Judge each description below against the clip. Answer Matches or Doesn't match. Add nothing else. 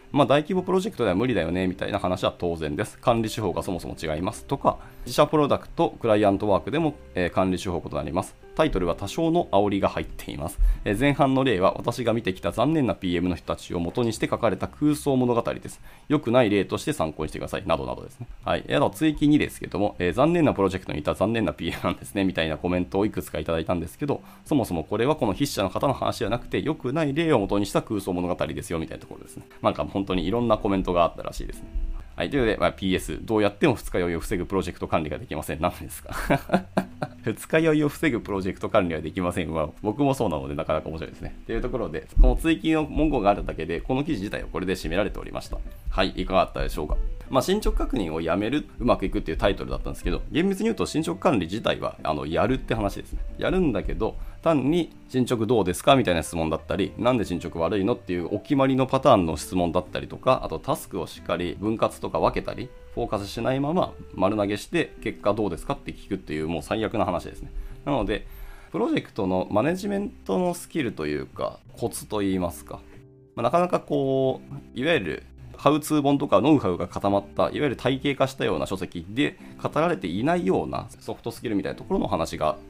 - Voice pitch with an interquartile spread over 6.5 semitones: Matches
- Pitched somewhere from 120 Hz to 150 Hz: Doesn't match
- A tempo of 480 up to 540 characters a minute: Matches